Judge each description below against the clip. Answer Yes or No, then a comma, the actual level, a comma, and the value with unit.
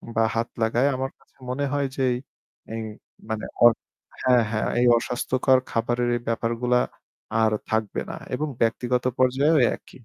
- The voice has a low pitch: Yes, low, 120 Hz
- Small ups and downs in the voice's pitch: Yes, narrow, 2.1 semitones